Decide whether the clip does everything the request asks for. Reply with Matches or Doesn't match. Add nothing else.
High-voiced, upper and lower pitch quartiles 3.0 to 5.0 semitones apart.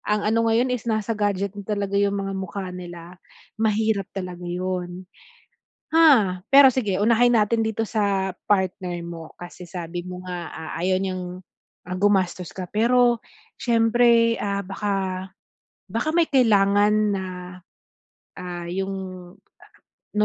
Matches